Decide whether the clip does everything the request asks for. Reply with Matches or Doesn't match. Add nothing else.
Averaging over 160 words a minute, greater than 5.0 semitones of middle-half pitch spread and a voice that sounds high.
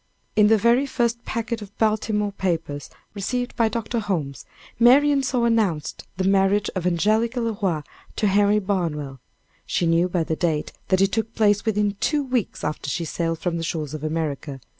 Matches